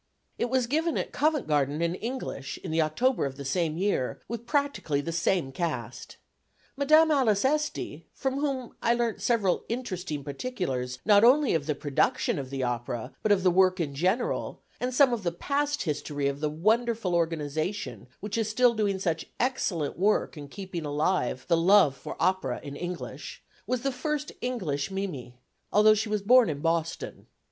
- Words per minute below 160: No, average, 175 wpm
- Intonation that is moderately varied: No, wide, 8.1 semitones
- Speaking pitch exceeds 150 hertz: Yes, high, 190 Hz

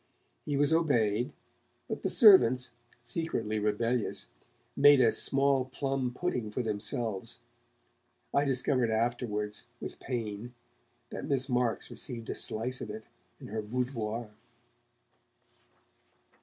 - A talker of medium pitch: No, low, 120 Hz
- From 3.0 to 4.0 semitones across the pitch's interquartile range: Yes, average, 3.5 semitones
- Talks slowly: Yes, slow, 115 wpm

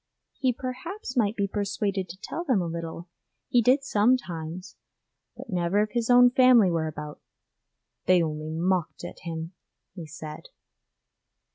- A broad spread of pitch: Yes, wide, 6.7 semitones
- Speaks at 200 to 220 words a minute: No, average, 145 wpm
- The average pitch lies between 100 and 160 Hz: No, high, 195 Hz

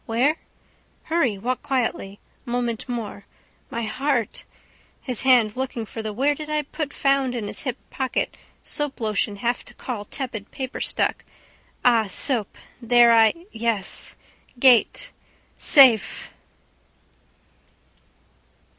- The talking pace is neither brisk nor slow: No, slow, 120 wpm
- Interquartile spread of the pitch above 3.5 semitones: No, average, 3.2 semitones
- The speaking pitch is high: Yes, high, 240 Hz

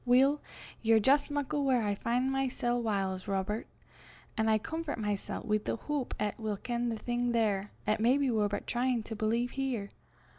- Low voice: No, high, 235 Hz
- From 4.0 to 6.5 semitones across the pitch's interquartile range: No, average, 3.5 semitones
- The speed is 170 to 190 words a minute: Yes, average, 180 wpm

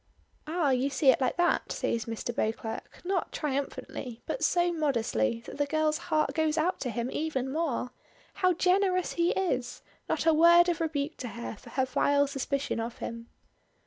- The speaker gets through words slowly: No, average, 175 wpm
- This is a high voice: Yes, very high, 285 Hz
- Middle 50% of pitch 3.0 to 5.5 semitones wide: Yes, average, 5.2 semitones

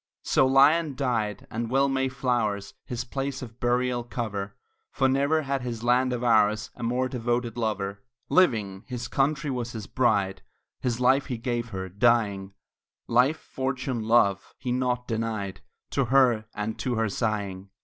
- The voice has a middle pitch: No, low, 120 Hz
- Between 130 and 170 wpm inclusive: Yes, average, 160 wpm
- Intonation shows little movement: No, average, 3.1 semitones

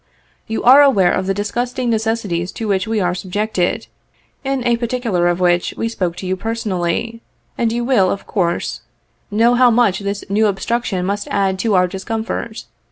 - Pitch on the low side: No, high, 210 Hz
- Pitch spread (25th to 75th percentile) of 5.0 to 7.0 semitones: No, average, 3.7 semitones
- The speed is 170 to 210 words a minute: Yes, average, 175 wpm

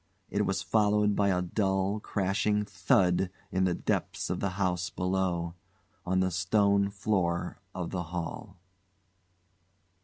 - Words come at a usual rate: No, slow, 130 wpm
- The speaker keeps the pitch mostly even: Yes, narrow, 1.8 semitones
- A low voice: Yes, very low, 95 Hz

